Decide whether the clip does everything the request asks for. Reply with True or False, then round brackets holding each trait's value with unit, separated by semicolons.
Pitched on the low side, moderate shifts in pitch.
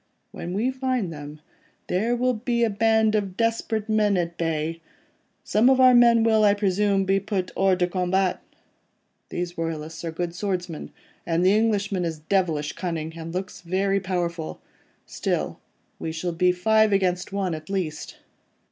False (190 Hz; 4.1 semitones)